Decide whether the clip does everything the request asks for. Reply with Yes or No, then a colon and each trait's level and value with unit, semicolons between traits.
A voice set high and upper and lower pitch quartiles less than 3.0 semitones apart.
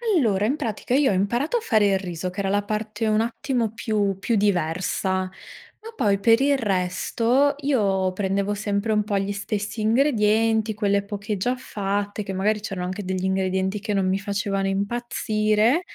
Yes: high, 205 Hz; narrow, 2.5 semitones